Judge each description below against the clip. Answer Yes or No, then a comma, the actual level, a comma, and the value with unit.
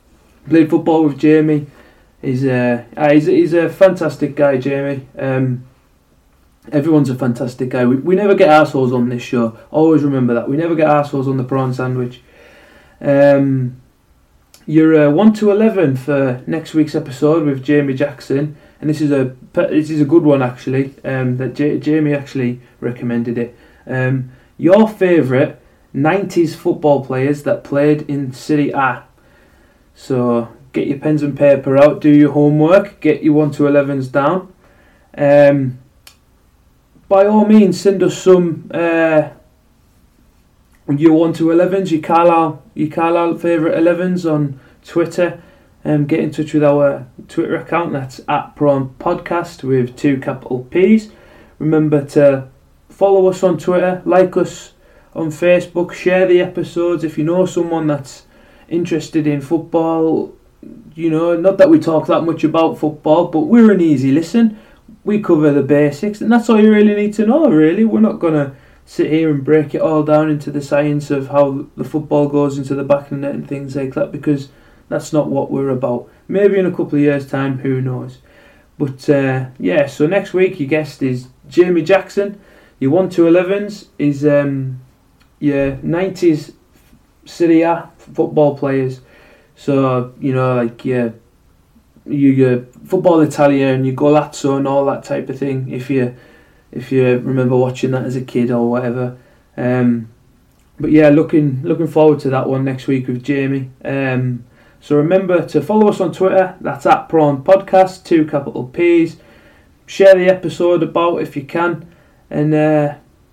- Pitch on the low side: No, medium, 145 Hz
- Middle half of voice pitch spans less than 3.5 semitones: No, average, 4.1 semitones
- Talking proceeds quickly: No, average, 165 wpm